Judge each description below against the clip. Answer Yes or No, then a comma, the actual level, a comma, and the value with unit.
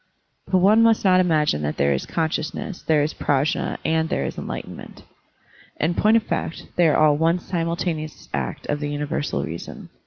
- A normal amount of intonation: Yes, average, 3.2 semitones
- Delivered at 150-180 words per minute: No, average, 195 wpm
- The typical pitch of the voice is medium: Yes, medium, 160 Hz